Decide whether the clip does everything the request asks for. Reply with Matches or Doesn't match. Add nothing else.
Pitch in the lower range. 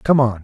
Matches